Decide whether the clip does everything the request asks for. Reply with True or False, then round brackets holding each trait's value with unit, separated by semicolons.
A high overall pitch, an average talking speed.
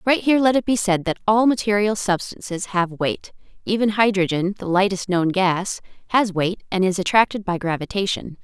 True (195 Hz; 180 wpm)